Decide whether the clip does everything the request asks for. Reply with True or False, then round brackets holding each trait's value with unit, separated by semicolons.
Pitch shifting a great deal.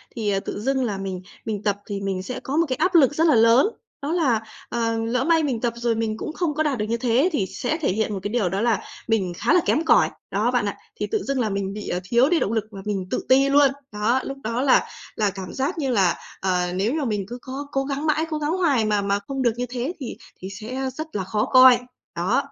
False (5.0 semitones)